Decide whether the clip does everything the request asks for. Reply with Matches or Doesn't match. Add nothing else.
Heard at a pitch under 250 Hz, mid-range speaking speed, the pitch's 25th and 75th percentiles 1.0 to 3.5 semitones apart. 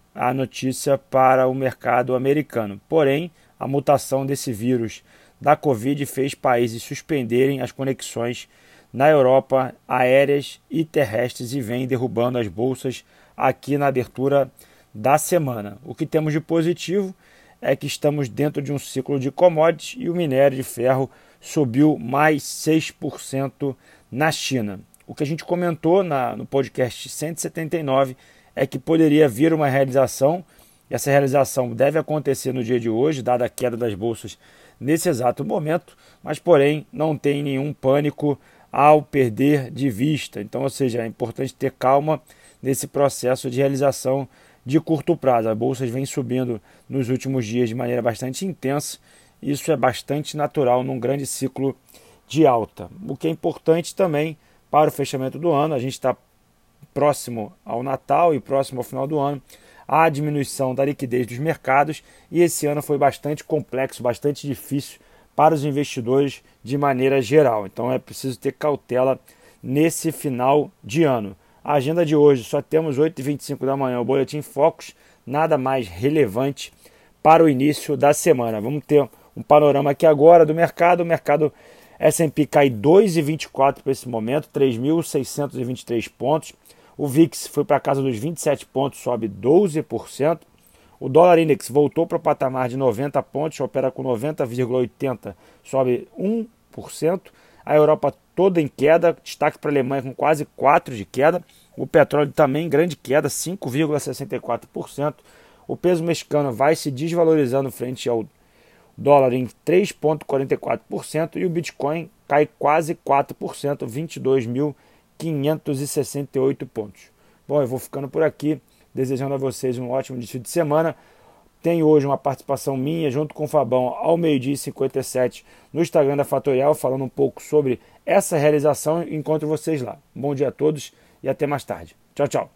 Matches